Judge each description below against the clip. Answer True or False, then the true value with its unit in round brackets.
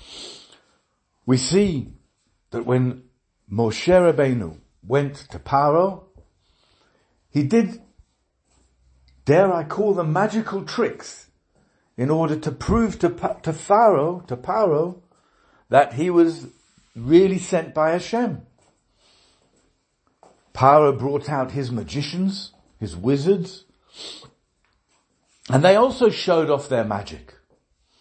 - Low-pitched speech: False (150 Hz)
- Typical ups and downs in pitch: False (6.8 semitones)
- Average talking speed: False (100 wpm)